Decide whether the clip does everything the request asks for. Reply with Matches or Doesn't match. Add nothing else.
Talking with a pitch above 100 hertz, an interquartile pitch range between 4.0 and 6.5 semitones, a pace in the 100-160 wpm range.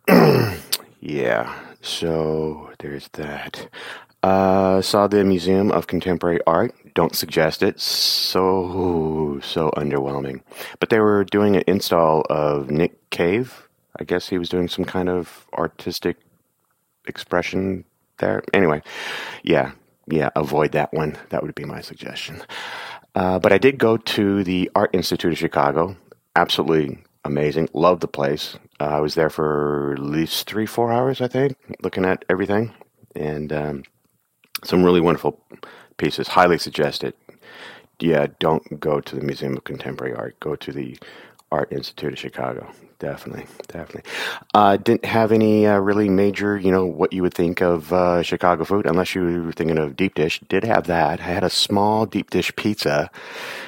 Doesn't match